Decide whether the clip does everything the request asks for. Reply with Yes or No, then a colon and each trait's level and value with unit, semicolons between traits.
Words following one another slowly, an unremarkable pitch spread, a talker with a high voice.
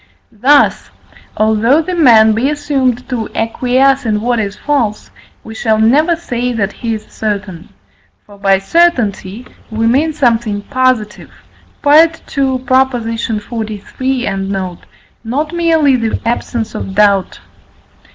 Yes: slow, 120 wpm; average, 4.0 semitones; high, 235 Hz